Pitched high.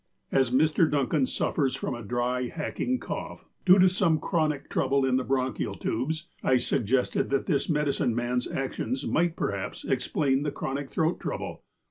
No: low, 135 Hz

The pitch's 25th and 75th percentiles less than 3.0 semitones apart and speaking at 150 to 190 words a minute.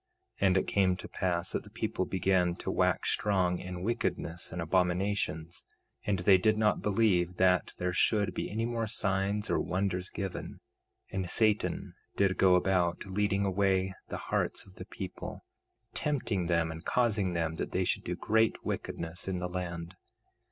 Yes: narrow, 2.4 semitones; average, 170 wpm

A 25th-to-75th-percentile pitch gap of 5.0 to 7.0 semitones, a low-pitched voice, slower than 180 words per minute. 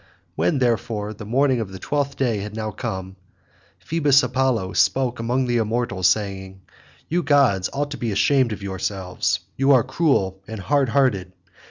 Yes: wide, 5.4 semitones; low, 115 Hz; average, 165 wpm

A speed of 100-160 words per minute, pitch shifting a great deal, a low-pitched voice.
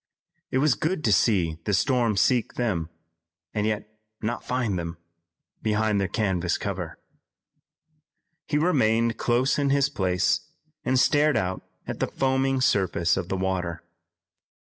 Yes: average, 140 wpm; wide, 5.7 semitones; low, 110 Hz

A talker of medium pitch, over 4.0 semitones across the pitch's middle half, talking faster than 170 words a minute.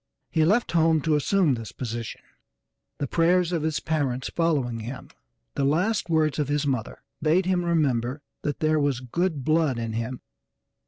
No: medium, 150 Hz; average, 4.4 semitones; average, 165 wpm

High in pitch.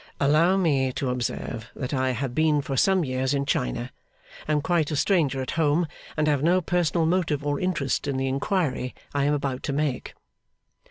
No: medium, 145 Hz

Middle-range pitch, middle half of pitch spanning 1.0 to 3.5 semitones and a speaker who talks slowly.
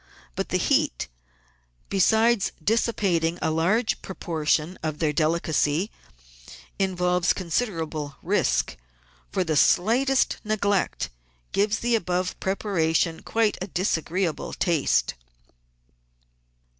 No: medium, 180 Hz; average, 4.3 semitones; slow, 100 wpm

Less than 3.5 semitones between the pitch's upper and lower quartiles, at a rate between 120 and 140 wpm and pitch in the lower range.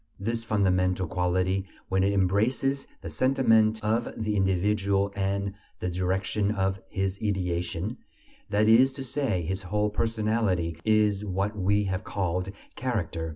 Yes: narrow, 2.6 semitones; slow, 135 wpm; low, 100 Hz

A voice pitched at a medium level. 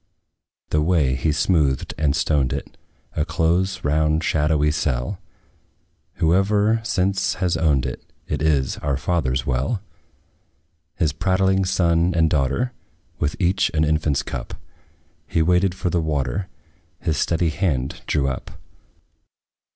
No: very low, 80 Hz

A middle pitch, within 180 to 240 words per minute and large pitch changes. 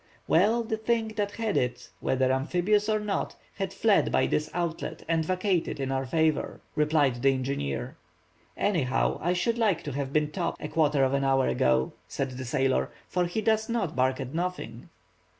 Yes: medium, 160 Hz; average, 185 wpm; wide, 7.1 semitones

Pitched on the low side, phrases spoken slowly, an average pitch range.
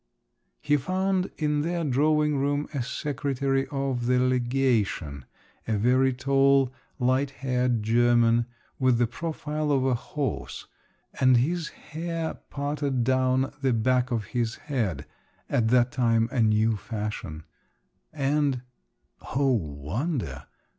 Yes: low, 130 Hz; slow, 120 wpm; average, 3.2 semitones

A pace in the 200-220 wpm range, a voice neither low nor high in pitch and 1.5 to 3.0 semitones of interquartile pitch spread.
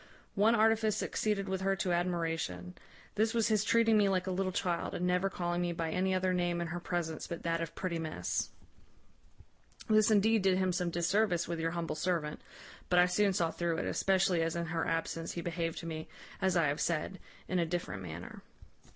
Yes: fast, 205 wpm; medium, 180 Hz; narrow, 2.5 semitones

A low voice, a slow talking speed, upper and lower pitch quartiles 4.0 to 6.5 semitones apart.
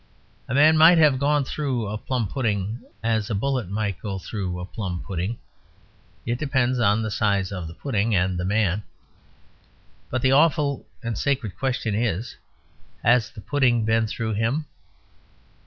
No: low, 115 Hz; average, 160 wpm; average, 4.6 semitones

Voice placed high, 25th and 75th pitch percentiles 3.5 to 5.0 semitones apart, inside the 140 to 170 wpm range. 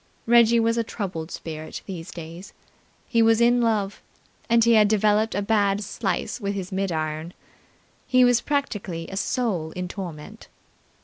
Yes: high, 205 Hz; average, 4.4 semitones; average, 160 wpm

